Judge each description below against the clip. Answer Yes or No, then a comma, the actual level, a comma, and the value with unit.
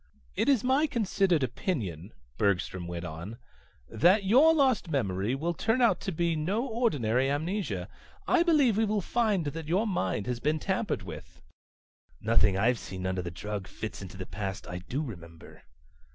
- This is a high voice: No, medium, 145 Hz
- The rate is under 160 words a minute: No, average, 165 wpm